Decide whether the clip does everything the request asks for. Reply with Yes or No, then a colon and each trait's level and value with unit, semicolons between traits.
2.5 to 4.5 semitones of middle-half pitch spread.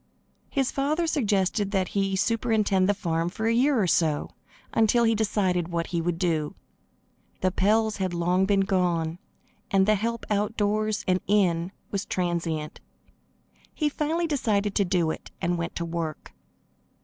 Yes: average, 3.9 semitones